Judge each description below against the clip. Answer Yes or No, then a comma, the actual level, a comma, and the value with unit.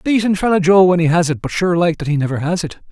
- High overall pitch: No, medium, 175 Hz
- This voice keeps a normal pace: No, fast, 310 wpm